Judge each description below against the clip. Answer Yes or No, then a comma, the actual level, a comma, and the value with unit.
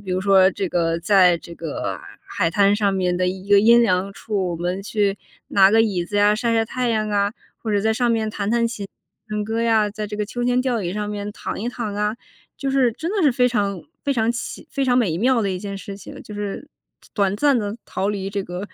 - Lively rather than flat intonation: No, average, 2.9 semitones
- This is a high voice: Yes, high, 205 Hz